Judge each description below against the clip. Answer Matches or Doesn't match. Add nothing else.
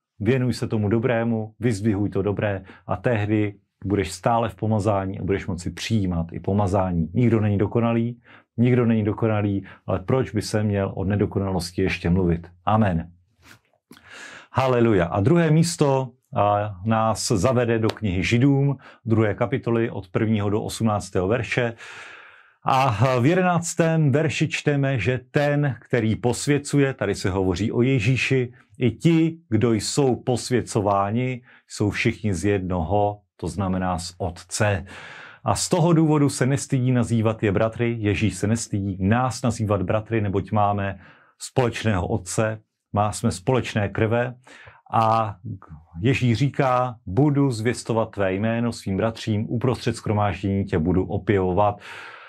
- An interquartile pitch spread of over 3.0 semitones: Matches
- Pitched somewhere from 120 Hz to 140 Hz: Doesn't match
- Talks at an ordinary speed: Matches